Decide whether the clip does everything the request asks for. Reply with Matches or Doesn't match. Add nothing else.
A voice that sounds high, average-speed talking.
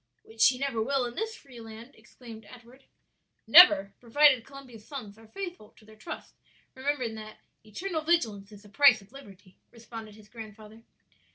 Matches